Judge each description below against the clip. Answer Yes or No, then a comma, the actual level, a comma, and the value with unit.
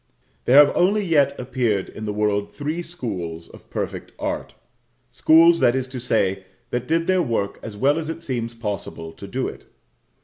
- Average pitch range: No, wide, 7.2 semitones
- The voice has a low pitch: Yes, low, 125 Hz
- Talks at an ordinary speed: Yes, average, 180 wpm